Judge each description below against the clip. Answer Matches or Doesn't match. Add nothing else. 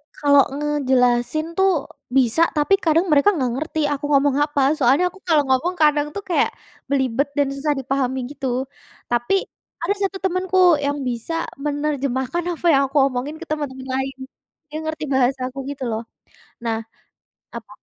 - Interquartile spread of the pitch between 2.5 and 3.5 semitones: Matches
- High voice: Matches